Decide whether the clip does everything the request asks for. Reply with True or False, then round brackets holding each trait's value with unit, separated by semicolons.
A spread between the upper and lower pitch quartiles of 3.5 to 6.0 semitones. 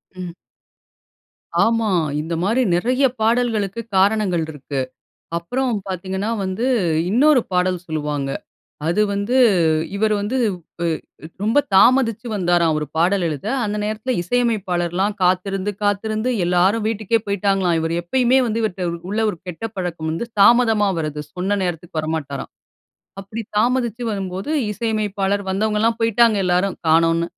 True (4.1 semitones)